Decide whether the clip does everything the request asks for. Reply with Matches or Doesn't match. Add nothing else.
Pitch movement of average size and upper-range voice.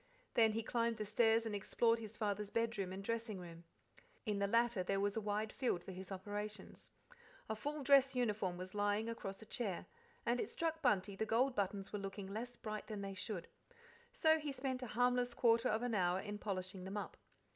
Matches